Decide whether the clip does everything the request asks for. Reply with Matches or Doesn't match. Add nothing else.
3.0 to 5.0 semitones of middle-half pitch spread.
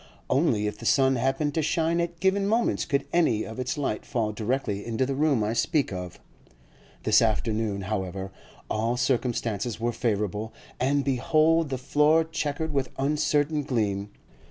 Doesn't match